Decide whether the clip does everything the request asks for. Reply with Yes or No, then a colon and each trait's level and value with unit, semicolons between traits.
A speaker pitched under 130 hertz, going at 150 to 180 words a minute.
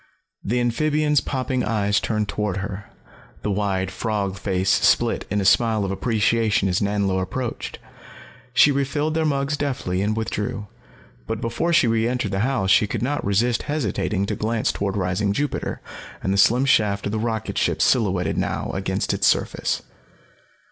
Yes: low, 110 Hz; average, 160 wpm